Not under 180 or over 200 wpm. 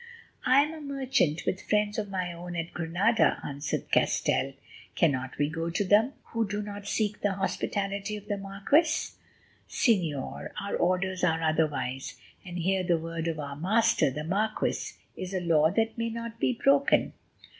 No: average, 165 wpm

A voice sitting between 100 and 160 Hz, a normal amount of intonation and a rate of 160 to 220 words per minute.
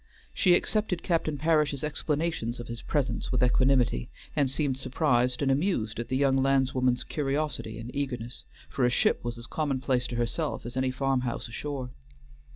Yes: low, 135 Hz; average, 3.1 semitones; average, 165 wpm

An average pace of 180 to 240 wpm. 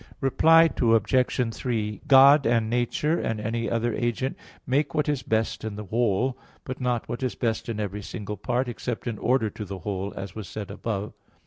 Yes: average, 195 wpm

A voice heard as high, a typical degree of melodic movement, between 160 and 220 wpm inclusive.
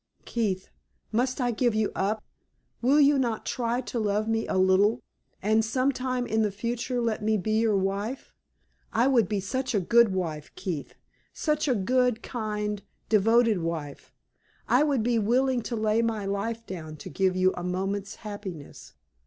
Yes: high, 220 Hz; average, 3.6 semitones; average, 170 wpm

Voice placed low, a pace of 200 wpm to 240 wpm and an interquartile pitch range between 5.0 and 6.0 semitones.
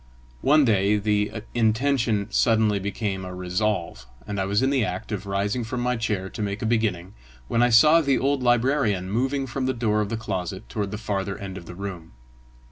No: low, 105 Hz; fast, 205 wpm; average, 3.7 semitones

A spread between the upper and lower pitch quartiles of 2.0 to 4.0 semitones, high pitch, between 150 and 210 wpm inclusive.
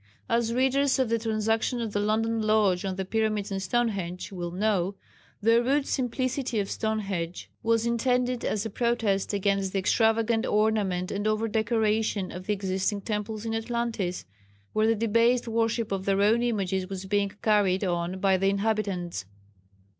Yes: average, 2.8 semitones; high, 215 Hz; average, 160 wpm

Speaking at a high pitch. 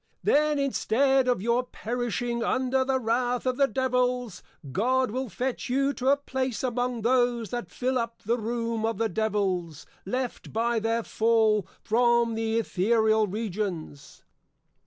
Yes: high, 235 Hz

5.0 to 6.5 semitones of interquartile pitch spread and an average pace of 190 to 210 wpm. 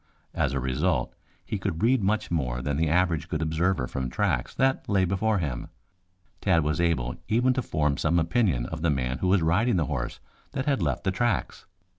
Yes: wide, 5.5 semitones; average, 200 wpm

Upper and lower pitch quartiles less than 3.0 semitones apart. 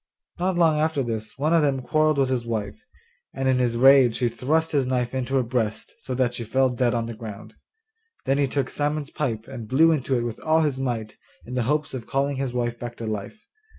No: average, 3.3 semitones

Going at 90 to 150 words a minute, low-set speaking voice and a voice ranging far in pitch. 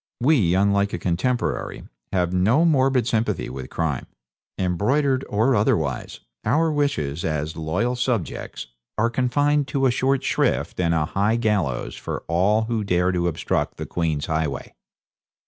Yes: average, 145 wpm; low, 100 Hz; wide, 7.0 semitones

